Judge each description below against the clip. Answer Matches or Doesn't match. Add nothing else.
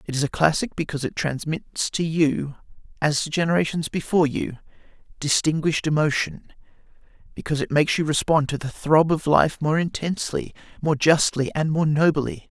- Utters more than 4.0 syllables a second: Matches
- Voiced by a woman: Doesn't match